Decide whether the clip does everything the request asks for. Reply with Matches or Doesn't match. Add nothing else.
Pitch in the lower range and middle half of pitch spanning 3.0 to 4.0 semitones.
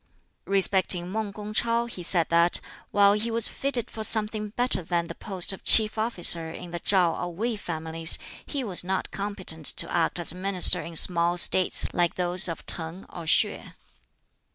Doesn't match